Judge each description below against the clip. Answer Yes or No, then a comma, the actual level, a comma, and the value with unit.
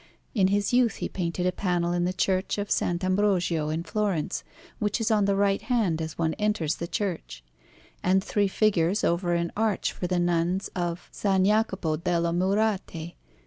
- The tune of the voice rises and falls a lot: No, average, 3.1 semitones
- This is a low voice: No, medium, 185 Hz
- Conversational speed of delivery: Yes, average, 180 wpm